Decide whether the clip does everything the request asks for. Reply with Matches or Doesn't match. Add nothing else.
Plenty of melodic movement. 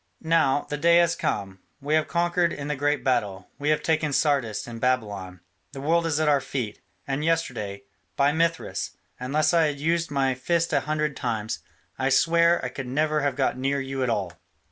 Doesn't match